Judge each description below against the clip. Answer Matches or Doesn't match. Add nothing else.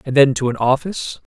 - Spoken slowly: Doesn't match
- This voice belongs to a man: Matches